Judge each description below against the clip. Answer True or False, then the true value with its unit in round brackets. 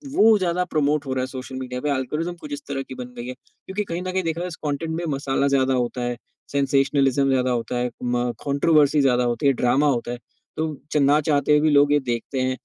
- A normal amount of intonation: True (3.2 semitones)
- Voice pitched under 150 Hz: True (140 Hz)